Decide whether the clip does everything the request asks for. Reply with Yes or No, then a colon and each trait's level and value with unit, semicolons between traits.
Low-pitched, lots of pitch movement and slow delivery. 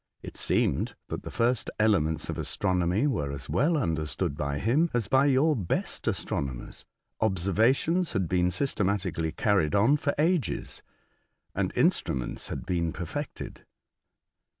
Yes: low, 100 Hz; wide, 8.4 semitones; slow, 130 wpm